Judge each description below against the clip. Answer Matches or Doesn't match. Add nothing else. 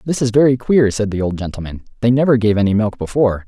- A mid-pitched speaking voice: Doesn't match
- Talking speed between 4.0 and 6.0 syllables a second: Doesn't match